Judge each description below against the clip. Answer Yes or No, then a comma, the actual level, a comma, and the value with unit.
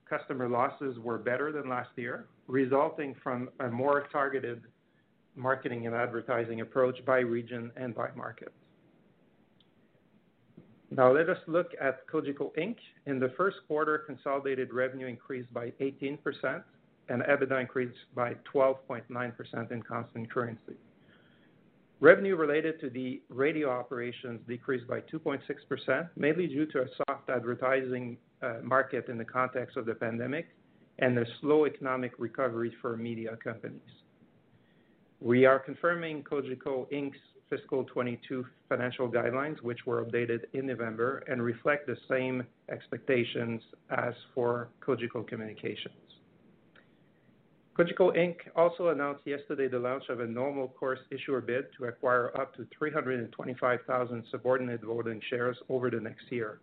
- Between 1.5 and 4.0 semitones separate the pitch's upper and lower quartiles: Yes, average, 2.7 semitones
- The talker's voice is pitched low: Yes, low, 130 Hz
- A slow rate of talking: Yes, slow, 130 wpm